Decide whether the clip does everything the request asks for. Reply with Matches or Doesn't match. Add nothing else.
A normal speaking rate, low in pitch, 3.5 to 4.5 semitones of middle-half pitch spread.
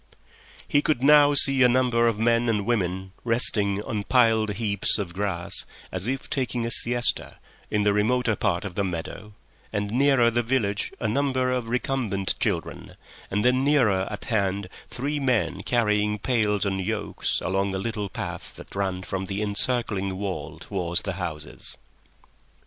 Matches